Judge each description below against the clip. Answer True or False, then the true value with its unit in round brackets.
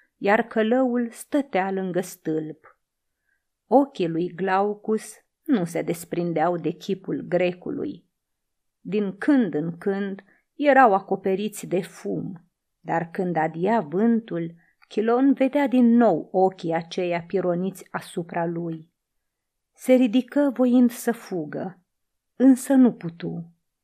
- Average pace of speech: False (110 wpm)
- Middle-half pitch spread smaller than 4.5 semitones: False (5.6 semitones)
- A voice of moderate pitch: False (195 Hz)